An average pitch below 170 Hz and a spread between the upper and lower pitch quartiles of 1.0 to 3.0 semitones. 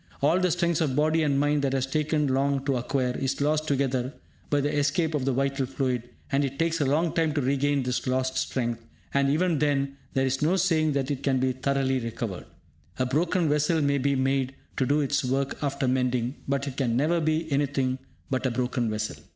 Yes: medium, 140 Hz; narrow, 2.4 semitones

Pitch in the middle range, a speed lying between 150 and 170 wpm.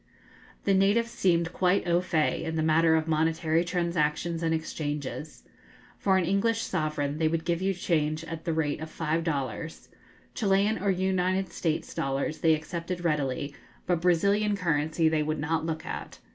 Yes: medium, 165 Hz; average, 165 wpm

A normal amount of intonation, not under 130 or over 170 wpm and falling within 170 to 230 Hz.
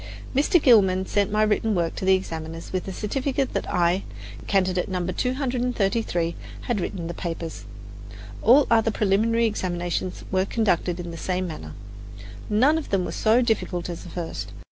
Yes: average, 4.5 semitones; average, 165 wpm; high, 190 Hz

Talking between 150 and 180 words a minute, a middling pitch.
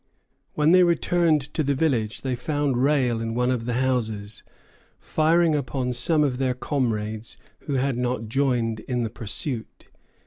No: average, 160 wpm; low, 125 Hz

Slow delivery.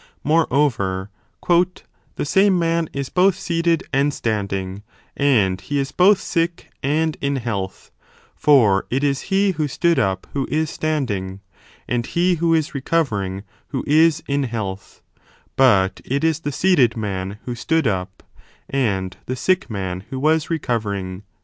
No: average, 150 wpm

